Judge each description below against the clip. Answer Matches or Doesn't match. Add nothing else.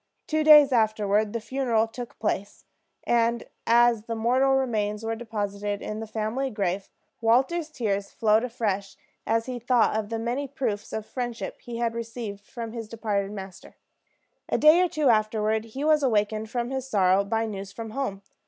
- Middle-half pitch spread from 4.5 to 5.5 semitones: Doesn't match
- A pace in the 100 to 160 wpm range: Doesn't match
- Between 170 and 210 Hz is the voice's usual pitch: Doesn't match